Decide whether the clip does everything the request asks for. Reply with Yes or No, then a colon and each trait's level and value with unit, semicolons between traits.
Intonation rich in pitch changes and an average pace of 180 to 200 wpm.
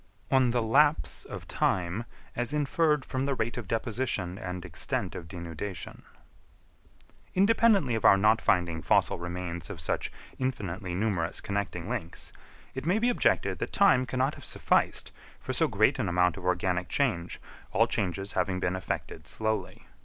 No: wide, 6.5 semitones; average, 155 wpm